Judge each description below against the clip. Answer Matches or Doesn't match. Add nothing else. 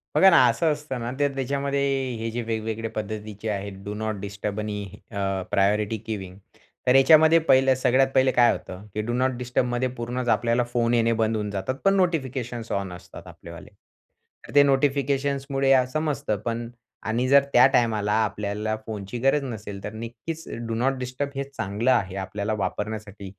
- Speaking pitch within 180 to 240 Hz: Doesn't match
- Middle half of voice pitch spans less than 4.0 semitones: Doesn't match